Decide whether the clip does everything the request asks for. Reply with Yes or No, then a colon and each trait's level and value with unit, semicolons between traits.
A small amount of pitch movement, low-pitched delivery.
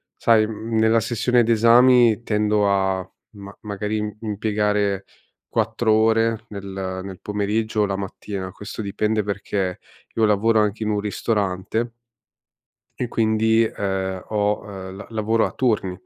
Yes: narrow, 2.0 semitones; low, 105 Hz